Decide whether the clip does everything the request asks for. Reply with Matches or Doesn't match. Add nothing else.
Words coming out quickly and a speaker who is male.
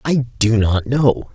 Doesn't match